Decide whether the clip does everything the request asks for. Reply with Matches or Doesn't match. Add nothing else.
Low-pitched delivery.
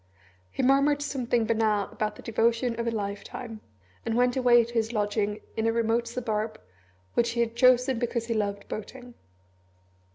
Doesn't match